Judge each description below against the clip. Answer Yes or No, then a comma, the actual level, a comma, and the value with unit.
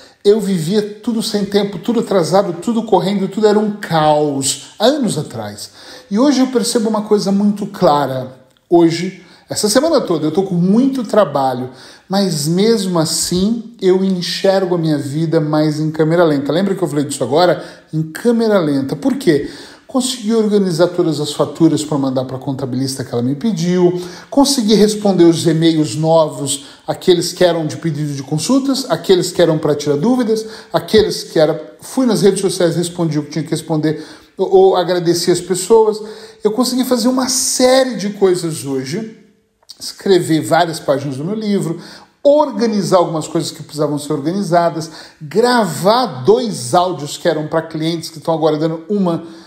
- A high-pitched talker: No, medium, 175 Hz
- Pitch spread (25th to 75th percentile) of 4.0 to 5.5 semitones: Yes, average, 5.2 semitones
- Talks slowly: No, average, 165 wpm